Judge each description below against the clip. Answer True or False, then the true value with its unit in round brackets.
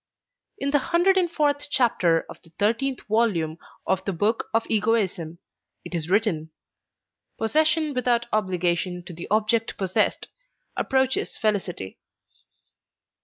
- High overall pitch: True (215 Hz)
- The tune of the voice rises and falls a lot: True (6.8 semitones)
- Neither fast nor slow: False (120 wpm)